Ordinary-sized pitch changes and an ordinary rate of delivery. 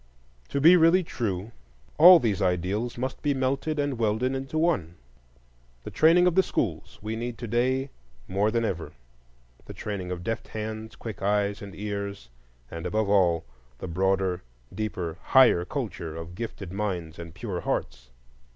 No: wide, 6.0 semitones; average, 155 wpm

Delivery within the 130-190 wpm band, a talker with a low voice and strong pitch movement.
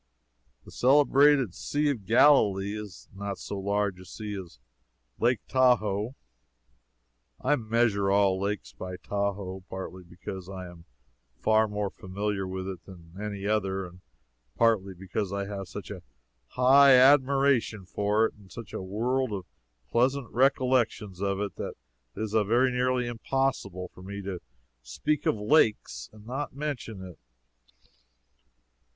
No: average, 145 wpm; low, 105 Hz; average, 4.5 semitones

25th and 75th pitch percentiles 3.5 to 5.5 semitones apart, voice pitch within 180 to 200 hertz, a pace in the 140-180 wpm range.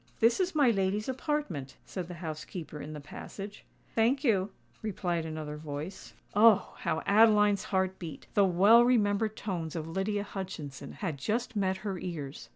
Yes: average, 4.9 semitones; high, 190 Hz; average, 155 wpm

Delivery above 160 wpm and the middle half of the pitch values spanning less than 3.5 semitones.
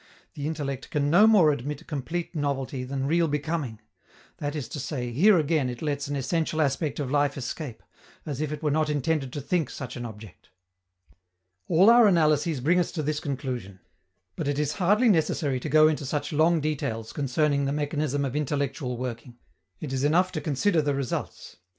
Yes: average, 185 wpm; average, 2.7 semitones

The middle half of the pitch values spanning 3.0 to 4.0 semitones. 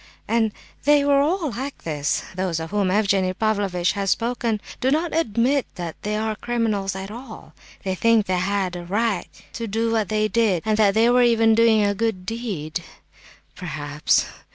Yes: average, 3.6 semitones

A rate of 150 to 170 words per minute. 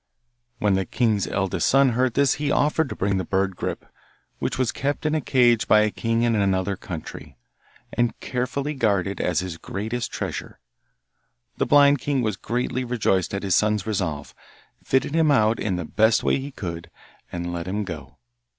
No: average, 180 wpm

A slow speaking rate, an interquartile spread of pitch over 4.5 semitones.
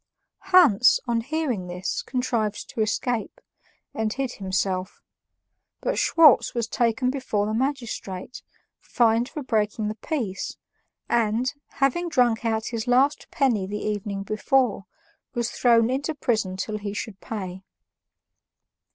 No: slow, 125 wpm; average, 3.6 semitones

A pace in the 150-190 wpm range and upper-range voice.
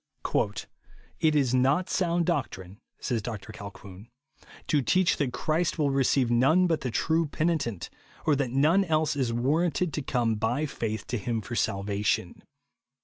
No: average, 155 wpm; low, 135 Hz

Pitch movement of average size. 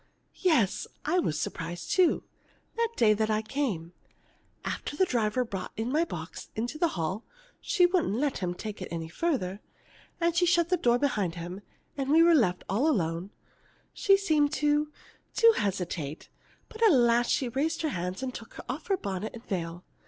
No: wide, 9.0 semitones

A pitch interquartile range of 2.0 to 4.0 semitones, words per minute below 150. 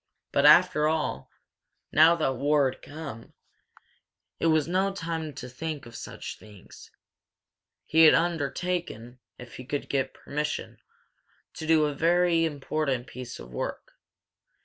Yes: average, 3.7 semitones; average, 140 wpm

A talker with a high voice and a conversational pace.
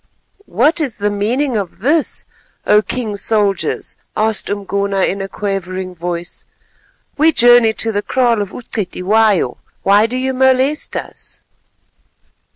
No: high, 210 Hz; slow, 130 wpm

